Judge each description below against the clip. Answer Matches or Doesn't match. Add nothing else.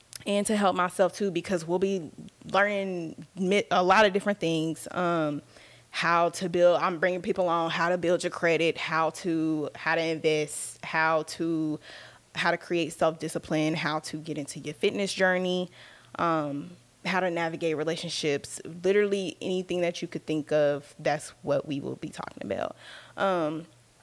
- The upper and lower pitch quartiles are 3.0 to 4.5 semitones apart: Doesn't match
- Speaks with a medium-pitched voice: Matches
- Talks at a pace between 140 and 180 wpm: Matches